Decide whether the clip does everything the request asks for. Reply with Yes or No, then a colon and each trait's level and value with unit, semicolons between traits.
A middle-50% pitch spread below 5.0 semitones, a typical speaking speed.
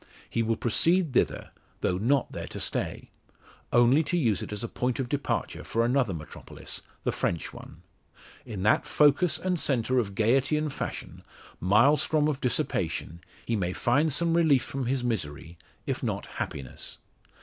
No: average, 5.3 semitones; average, 160 wpm